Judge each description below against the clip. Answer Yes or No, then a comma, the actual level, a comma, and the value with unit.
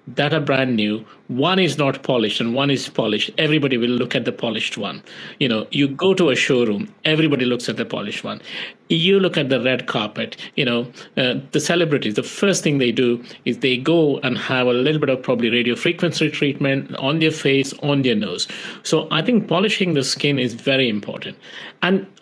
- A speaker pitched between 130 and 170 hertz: Yes, medium, 140 Hz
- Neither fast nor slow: No, fast, 210 wpm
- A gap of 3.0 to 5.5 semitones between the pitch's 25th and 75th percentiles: Yes, average, 4.6 semitones